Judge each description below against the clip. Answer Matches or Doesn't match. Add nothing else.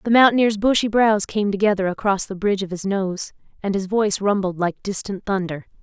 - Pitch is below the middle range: Doesn't match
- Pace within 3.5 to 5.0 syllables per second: Doesn't match